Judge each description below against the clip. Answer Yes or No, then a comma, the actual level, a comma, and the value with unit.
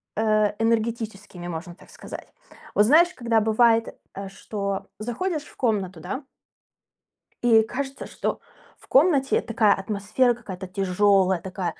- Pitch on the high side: Yes, high, 215 Hz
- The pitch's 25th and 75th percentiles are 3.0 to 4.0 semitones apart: Yes, average, 3.6 semitones